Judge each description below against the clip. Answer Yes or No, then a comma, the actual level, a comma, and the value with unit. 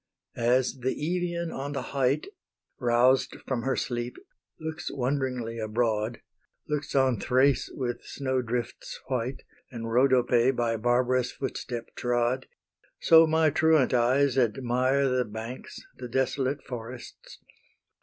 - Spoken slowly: Yes, slow, 120 wpm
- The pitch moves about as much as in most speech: No, narrow, 2.2 semitones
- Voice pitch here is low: Yes, low, 130 Hz